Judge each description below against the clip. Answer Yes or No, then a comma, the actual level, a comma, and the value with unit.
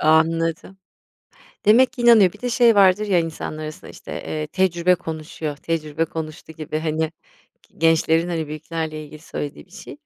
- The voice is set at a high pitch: No, medium, 165 Hz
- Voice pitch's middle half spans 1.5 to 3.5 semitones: Yes, average, 2.8 semitones